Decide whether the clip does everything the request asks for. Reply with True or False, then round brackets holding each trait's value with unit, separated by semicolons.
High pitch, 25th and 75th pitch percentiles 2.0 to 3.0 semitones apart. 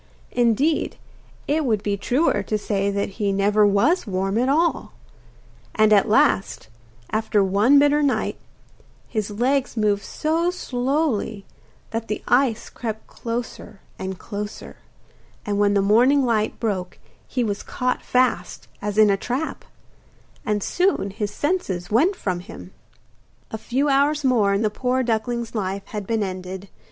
False (220 Hz; 4.3 semitones)